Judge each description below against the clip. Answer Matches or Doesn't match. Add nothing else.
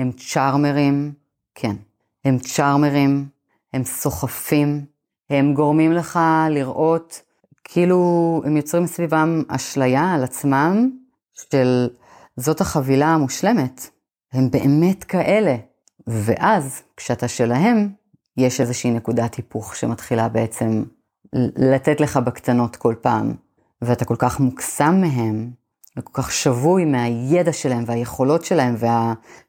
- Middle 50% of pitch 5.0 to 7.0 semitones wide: Doesn't match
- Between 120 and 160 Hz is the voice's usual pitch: Matches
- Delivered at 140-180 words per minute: Doesn't match